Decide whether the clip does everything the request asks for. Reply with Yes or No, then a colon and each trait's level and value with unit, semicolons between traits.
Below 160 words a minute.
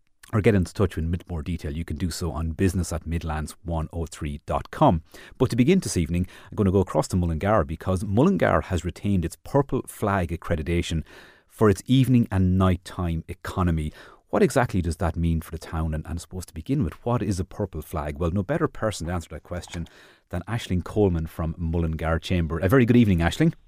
No: fast, 205 wpm